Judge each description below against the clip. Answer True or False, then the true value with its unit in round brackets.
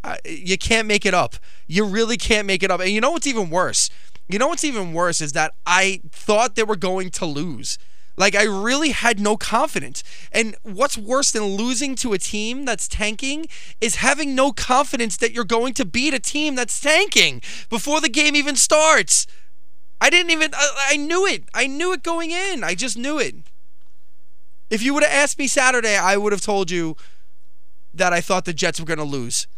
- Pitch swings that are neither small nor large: False (7.7 semitones)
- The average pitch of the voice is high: True (220 Hz)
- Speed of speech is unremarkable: False (210 wpm)